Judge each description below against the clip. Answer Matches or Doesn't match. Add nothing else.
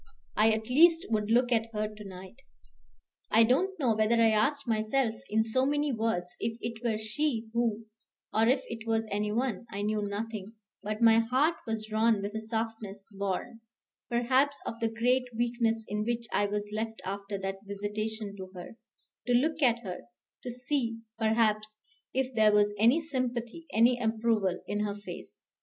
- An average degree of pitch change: Doesn't match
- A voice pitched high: Matches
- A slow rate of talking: Doesn't match